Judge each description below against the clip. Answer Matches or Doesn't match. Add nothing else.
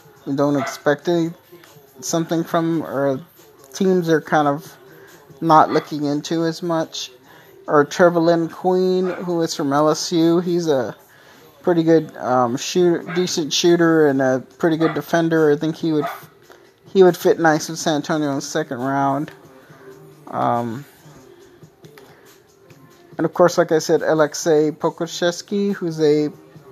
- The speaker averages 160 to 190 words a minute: Doesn't match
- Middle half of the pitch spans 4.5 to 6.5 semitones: Doesn't match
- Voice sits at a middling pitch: Matches